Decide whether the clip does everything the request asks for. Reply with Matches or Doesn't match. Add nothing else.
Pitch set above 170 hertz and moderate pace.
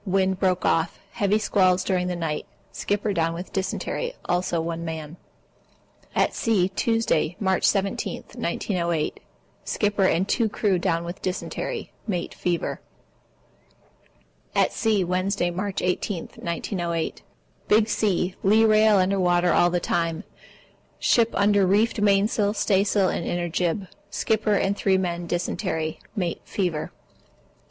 Doesn't match